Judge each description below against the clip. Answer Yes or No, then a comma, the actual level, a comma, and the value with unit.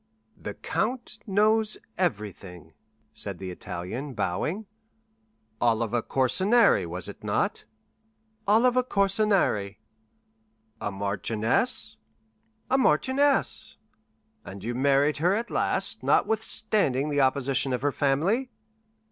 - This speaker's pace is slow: Yes, slow, 95 wpm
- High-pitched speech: No, medium, 140 Hz